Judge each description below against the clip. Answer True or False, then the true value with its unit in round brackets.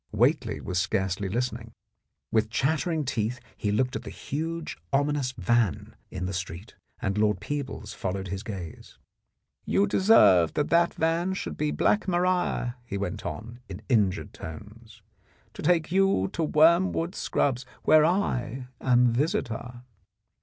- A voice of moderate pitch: False (120 Hz)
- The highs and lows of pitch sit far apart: True (7.6 semitones)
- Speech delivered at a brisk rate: False (140 wpm)